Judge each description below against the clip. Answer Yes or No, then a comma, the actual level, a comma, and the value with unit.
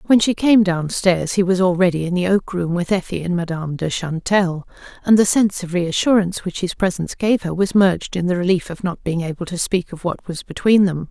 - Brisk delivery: Yes, fast, 230 wpm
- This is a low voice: No, medium, 180 Hz